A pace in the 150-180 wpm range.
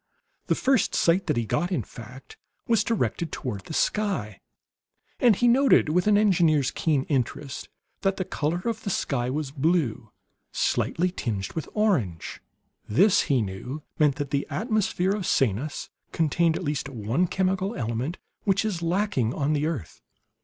Yes: average, 160 wpm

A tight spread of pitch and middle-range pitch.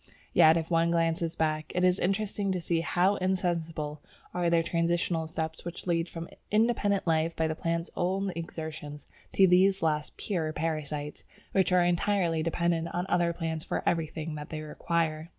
Yes: narrow, 2.0 semitones; medium, 170 Hz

